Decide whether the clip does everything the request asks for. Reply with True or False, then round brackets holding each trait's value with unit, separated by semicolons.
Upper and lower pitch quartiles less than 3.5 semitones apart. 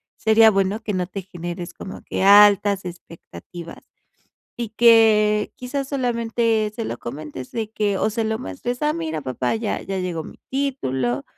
False (4.5 semitones)